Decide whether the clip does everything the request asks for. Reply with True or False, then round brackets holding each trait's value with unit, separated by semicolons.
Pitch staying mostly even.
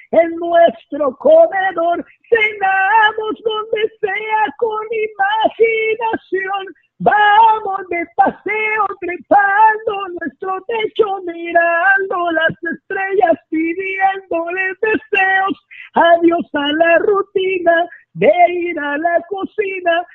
False (3.9 semitones)